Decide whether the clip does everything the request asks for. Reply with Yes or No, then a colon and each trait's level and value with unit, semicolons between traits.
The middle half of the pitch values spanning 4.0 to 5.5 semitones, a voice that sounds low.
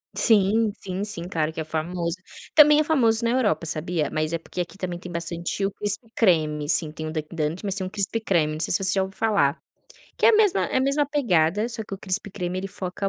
No: average, 4.7 semitones; high, 190 Hz